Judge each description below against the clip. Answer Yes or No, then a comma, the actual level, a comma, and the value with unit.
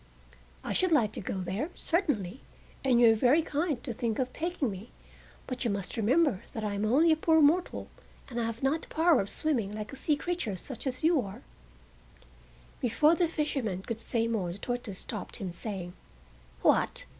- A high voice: Yes, high, 245 Hz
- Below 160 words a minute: No, average, 190 wpm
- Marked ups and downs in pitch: Yes, wide, 6.4 semitones